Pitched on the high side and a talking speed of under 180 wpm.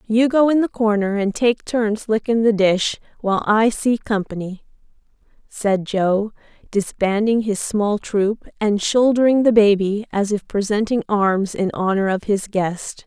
Yes: high, 210 Hz; average, 155 wpm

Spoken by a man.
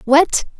No: female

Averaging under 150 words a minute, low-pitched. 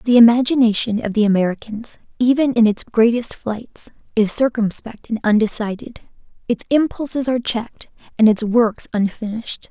No: slow, 135 wpm; high, 230 Hz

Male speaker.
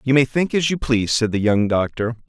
Yes: male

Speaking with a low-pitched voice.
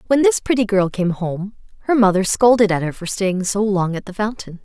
No: high, 200 Hz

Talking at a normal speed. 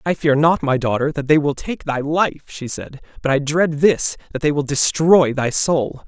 No: fast, 215 wpm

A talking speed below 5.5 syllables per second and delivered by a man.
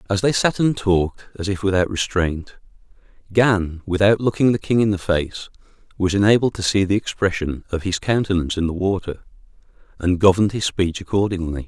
No: 5.6 syllables/s; male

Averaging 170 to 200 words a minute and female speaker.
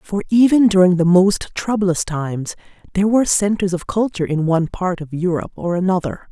Yes: average, 180 wpm; female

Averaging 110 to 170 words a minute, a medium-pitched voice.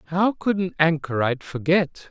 Yes: average, 140 wpm; medium, 165 Hz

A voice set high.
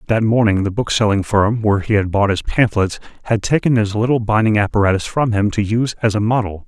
No: low, 105 Hz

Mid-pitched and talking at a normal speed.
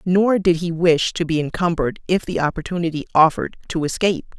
Yes: medium, 170 Hz; average, 180 wpm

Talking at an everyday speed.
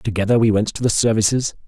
No: fast, 215 wpm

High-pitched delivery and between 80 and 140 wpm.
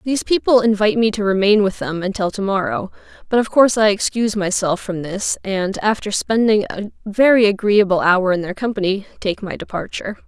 No: high, 205 Hz; average, 185 wpm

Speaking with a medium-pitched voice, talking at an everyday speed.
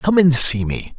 No: medium, 145 Hz; fast, 245 wpm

